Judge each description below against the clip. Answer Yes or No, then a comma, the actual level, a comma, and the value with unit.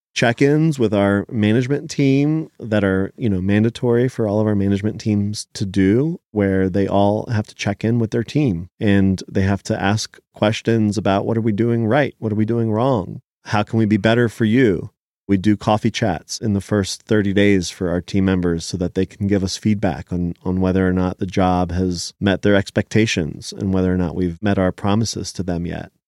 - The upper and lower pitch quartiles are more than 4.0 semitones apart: No, average, 2.8 semitones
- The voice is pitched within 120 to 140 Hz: No, low, 105 Hz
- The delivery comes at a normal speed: No, fast, 215 wpm